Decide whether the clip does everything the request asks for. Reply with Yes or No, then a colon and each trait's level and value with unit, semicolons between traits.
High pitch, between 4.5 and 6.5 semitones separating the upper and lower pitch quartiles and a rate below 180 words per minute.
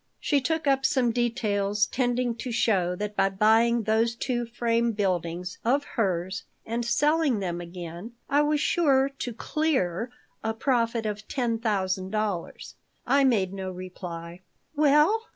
Yes: high, 230 Hz; average, 5.2 semitones; average, 145 wpm